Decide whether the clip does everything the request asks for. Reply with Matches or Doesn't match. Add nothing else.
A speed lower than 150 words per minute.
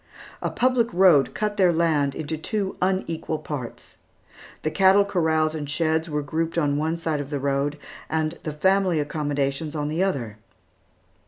Doesn't match